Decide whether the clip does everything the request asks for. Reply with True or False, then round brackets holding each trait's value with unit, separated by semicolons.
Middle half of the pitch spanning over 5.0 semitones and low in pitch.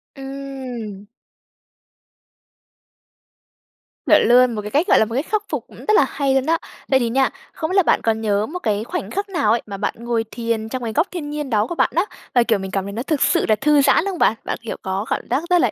False (5.4 semitones; 250 Hz)